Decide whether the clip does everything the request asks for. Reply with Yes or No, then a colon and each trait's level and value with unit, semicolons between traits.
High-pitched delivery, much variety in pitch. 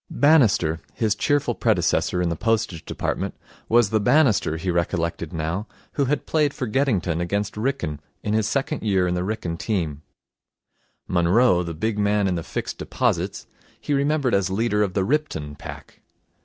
No: low, 105 Hz; wide, 5.9 semitones